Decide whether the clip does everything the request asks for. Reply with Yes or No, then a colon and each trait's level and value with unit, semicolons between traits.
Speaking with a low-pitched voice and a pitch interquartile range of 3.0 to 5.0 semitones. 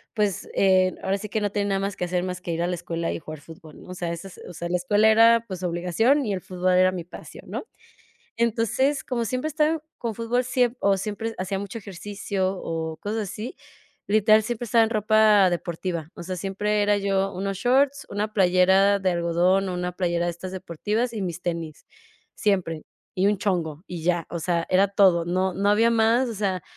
No: high, 195 Hz; average, 3.4 semitones